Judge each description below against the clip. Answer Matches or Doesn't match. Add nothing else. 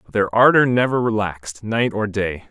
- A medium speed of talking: Matches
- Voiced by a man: Matches